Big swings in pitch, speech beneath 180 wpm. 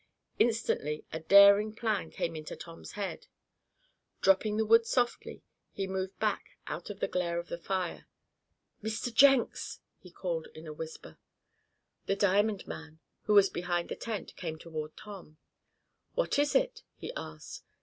No: average, 4.3 semitones; average, 150 wpm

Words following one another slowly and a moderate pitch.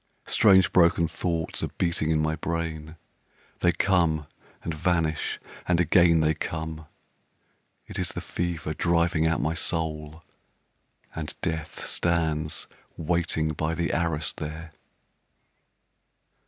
No: slow, 115 wpm; very low, 80 Hz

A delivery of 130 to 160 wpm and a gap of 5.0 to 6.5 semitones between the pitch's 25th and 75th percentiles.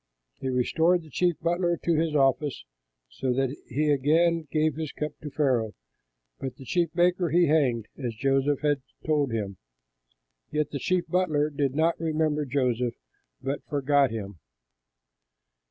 No: average, 150 wpm; average, 3.4 semitones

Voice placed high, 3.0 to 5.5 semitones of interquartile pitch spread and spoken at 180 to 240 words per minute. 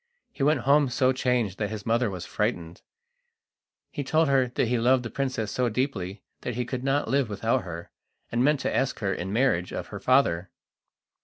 No: low, 125 Hz; average, 4.5 semitones; average, 190 wpm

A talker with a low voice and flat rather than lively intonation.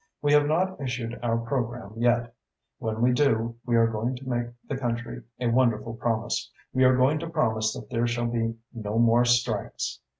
Yes: low, 120 Hz; narrow, 1.9 semitones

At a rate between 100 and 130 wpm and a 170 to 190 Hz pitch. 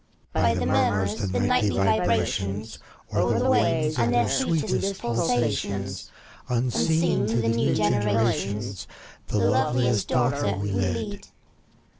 No: slow, 115 wpm; low, 110 Hz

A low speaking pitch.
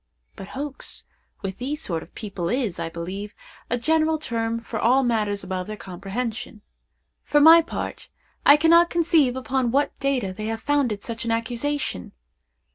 No: high, 235 Hz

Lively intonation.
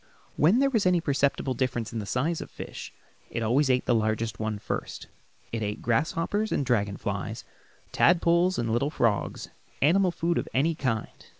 Yes: wide, 6.7 semitones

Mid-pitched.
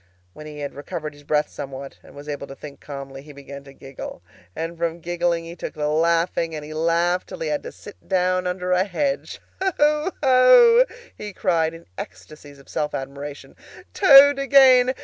Yes: medium, 165 Hz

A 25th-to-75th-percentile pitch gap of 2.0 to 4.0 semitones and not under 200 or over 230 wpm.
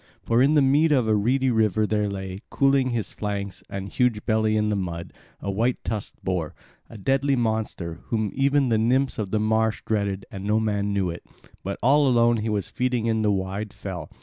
Yes: average, 3.7 semitones; fast, 205 wpm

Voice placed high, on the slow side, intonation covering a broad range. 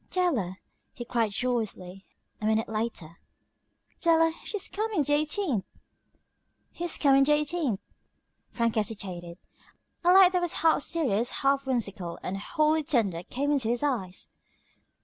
Yes: very high, 255 Hz; slow, 130 wpm; wide, 7.0 semitones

